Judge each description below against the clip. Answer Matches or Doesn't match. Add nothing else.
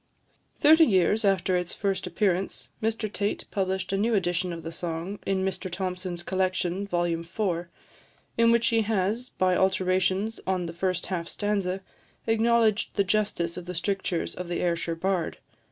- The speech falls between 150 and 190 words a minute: Matches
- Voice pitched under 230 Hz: Matches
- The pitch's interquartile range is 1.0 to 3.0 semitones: Matches